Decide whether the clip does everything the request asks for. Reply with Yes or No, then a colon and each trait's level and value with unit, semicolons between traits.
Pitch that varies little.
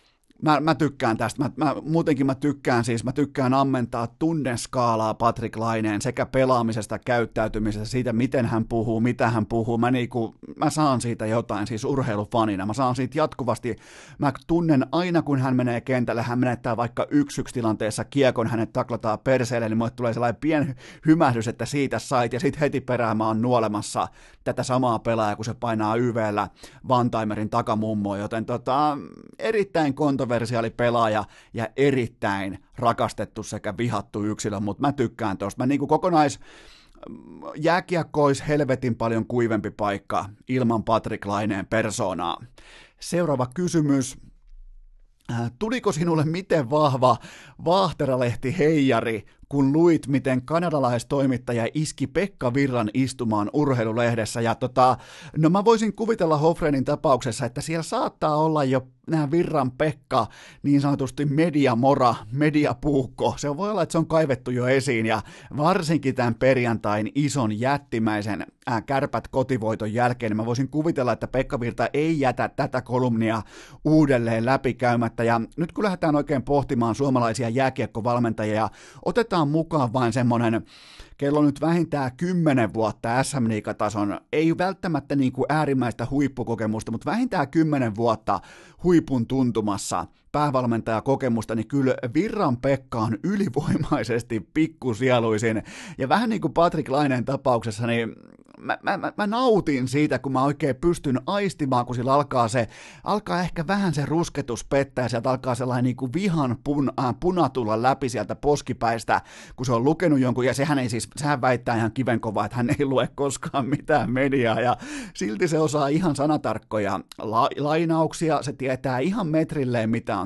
No: average, 4.3 semitones